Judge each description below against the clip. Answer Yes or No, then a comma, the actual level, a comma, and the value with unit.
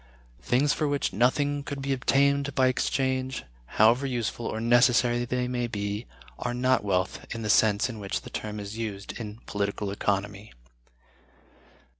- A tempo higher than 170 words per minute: No, average, 155 wpm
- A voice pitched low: Yes, low, 120 Hz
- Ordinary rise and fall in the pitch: Yes, average, 3.9 semitones